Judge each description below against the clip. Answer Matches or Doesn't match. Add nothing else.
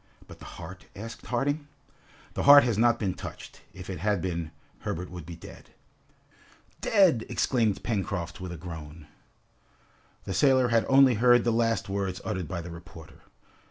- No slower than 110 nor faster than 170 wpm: Matches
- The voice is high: Doesn't match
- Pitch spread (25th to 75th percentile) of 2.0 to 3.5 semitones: Doesn't match